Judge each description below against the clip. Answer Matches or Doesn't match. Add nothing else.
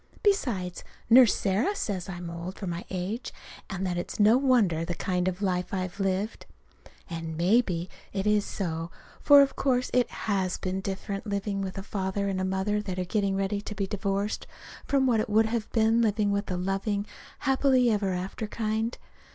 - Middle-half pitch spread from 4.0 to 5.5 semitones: Doesn't match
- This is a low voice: Doesn't match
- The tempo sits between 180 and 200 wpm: Matches